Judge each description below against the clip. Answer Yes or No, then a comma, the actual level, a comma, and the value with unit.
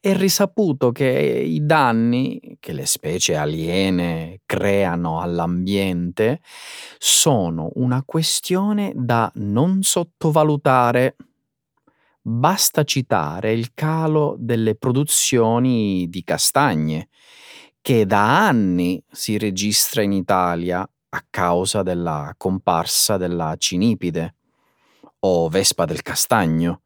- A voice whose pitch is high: No, low, 105 Hz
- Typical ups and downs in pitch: No, wide, 6.9 semitones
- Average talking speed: No, slow, 95 wpm